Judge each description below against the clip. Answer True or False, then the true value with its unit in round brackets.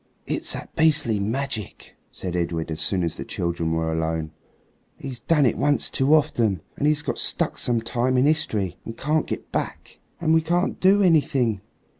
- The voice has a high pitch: False (120 Hz)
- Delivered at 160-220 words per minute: True (180 wpm)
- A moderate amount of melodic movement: False (9.0 semitones)